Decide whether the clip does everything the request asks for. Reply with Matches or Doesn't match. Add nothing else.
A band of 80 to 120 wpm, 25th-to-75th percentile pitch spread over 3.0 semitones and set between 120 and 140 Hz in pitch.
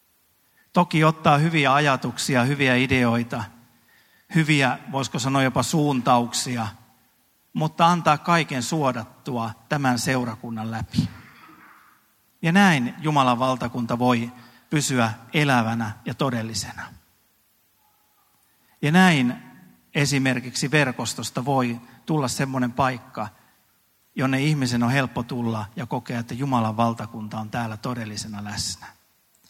Matches